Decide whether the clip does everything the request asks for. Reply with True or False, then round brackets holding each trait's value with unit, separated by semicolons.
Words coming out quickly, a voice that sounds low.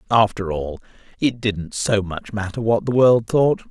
False (180 wpm; 105 Hz)